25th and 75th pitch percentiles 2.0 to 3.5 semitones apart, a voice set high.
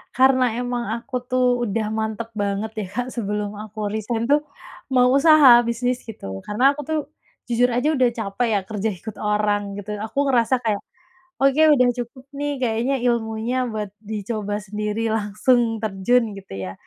Yes: average, 3.1 semitones; high, 225 Hz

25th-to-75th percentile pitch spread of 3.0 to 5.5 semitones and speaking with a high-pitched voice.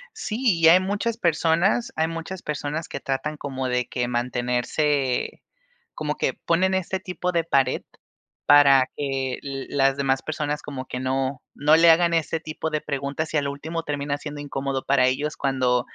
No: average, 3.5 semitones; medium, 145 Hz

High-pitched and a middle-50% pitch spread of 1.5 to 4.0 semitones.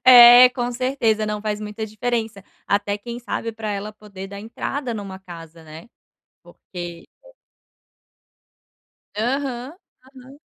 Yes: high, 220 Hz; average, 3.3 semitones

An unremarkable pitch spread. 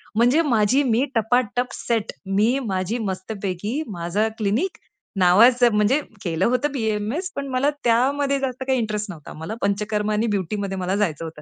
Yes: average, 4.1 semitones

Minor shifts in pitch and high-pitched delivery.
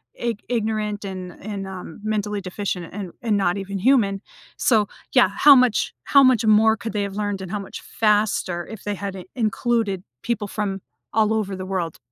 Yes: narrow, 2.2 semitones; high, 205 Hz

